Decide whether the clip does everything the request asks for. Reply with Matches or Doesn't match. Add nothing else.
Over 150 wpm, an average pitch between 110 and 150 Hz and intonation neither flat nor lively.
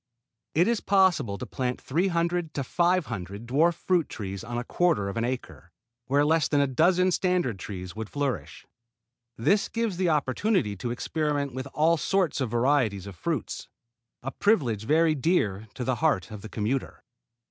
Doesn't match